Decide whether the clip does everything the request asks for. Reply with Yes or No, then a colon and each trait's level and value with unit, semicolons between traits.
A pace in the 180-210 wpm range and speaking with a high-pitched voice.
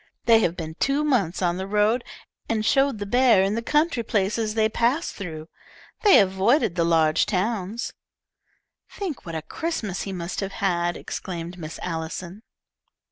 No: average, 160 wpm; high, 200 Hz